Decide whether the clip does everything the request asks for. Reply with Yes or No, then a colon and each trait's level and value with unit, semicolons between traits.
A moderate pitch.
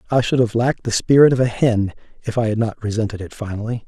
No: low, 115 Hz